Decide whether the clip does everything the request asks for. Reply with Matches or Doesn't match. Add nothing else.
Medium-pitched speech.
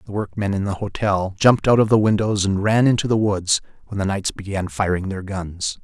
Doesn't match